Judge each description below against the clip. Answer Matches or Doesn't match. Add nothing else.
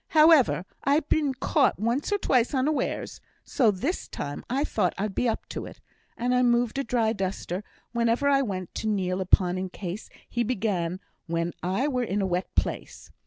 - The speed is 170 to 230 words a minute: Matches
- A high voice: Matches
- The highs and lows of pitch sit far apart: Matches